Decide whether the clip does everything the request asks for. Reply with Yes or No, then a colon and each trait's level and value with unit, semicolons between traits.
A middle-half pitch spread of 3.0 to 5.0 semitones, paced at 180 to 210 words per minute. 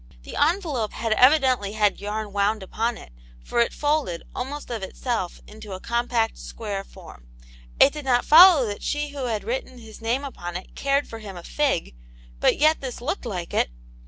No: wide, 5.4 semitones; average, 190 wpm